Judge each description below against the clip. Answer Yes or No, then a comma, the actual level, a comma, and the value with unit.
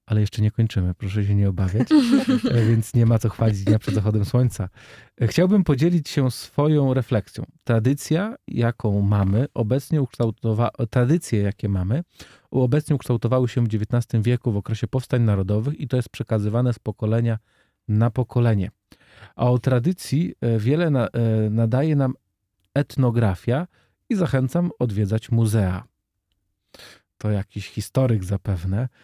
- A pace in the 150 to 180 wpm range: No, average, 130 wpm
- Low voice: Yes, low, 115 Hz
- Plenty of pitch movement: No, average, 3.7 semitones